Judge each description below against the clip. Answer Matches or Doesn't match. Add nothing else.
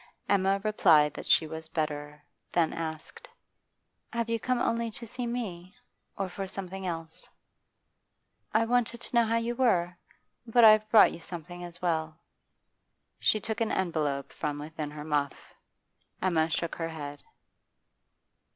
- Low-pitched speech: Doesn't match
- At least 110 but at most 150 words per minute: Matches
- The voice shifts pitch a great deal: Matches